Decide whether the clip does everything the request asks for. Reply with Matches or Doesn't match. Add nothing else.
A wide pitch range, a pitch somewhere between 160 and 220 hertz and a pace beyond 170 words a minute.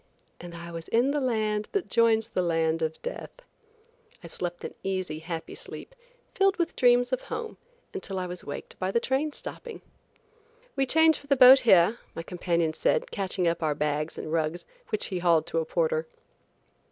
Matches